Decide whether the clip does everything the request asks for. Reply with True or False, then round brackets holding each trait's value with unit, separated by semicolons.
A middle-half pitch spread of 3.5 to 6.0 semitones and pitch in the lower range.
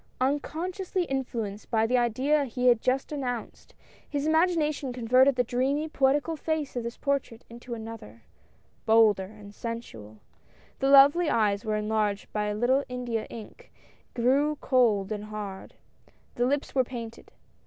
False (4.2 semitones; 245 Hz)